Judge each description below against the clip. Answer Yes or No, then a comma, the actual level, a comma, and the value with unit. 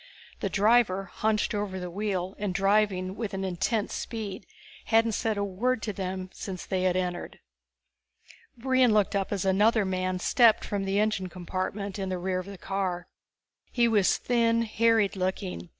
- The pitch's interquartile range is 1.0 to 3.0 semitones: Yes, average, 2.7 semitones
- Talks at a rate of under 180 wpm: Yes, average, 165 wpm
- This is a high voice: Yes, high, 195 Hz